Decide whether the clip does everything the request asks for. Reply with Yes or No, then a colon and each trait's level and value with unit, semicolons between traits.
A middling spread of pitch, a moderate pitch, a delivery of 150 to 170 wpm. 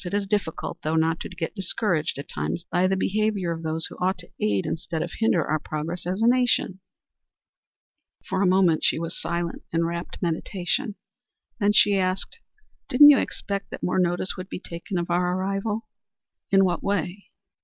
No: average, 3.1 semitones; medium, 180 Hz; average, 185 wpm